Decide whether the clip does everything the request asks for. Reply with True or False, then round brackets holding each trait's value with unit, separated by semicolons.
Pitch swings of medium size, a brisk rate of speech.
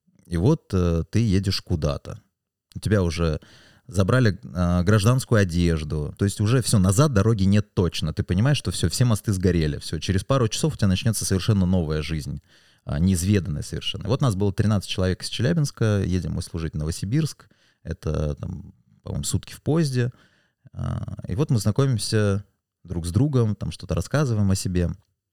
True (4.6 semitones; 175 wpm)